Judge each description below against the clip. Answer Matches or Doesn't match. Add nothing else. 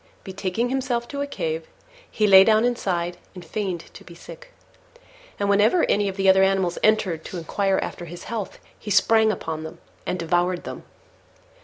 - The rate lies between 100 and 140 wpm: Doesn't match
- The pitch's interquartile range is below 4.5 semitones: Matches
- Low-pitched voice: Doesn't match